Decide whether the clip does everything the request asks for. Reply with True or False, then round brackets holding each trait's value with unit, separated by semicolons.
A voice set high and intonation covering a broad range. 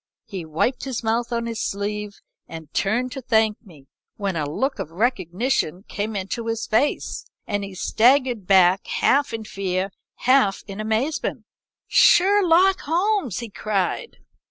False (220 Hz; 4.6 semitones)